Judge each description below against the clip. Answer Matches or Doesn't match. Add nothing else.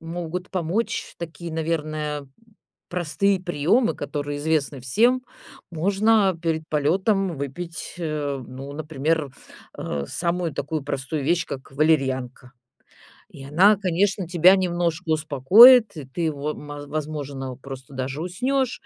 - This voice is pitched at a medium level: Matches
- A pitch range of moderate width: Matches